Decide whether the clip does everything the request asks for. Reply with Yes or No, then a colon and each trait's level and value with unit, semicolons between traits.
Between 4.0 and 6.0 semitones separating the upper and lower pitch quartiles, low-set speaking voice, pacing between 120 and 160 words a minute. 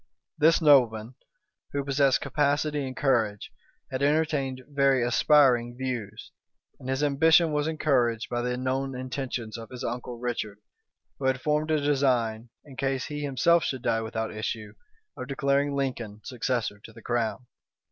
No: average, 3.1 semitones; low, 130 Hz; average, 150 wpm